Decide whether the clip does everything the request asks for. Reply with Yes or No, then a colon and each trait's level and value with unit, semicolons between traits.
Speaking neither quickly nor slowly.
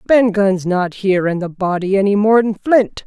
Yes: average, 195 wpm